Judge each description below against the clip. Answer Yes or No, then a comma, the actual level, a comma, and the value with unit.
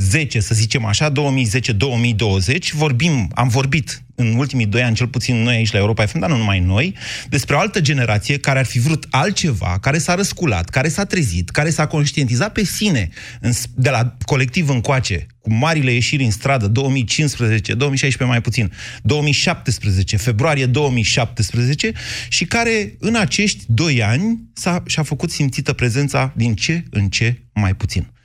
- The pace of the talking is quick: No, average, 160 wpm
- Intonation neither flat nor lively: Yes, average, 4.6 semitones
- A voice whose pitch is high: No, low, 130 Hz